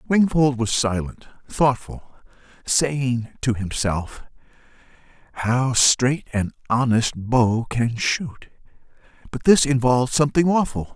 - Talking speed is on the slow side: Yes, slow, 95 wpm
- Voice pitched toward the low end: Yes, low, 125 Hz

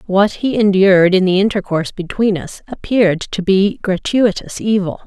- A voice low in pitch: No, high, 195 Hz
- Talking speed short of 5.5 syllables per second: Yes, 5.0 syllables/s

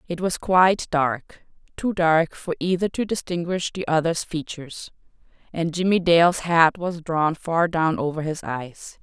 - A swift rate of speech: No, average, 155 wpm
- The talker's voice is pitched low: No, medium, 170 Hz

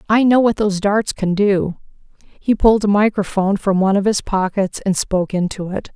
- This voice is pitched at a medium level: No, high, 200 Hz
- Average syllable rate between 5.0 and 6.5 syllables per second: Yes, 5.5 syllables/s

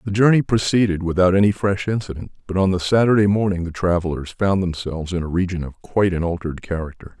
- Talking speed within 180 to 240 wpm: Yes, average, 200 wpm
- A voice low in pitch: Yes, very low, 95 Hz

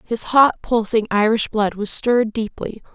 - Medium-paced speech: Yes, average, 165 wpm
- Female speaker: Yes, female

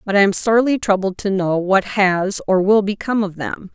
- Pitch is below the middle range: No, high, 200 Hz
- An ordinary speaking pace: No, fast, 225 wpm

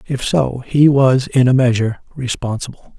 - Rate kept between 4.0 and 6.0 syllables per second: Yes, 4.8 syllables/s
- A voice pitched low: Yes, low, 125 Hz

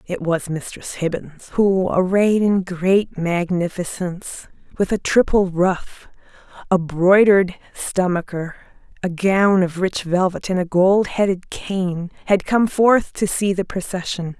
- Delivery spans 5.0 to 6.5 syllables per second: No, 3.9 syllables/s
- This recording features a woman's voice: Yes, female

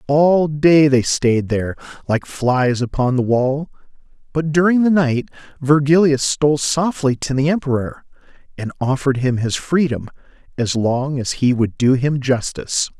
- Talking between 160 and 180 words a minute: No, average, 150 wpm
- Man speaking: Yes, male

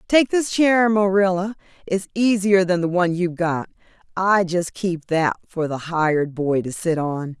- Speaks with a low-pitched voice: No, medium, 180 Hz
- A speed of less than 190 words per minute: Yes, average, 180 wpm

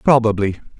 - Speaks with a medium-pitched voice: No, low, 110 Hz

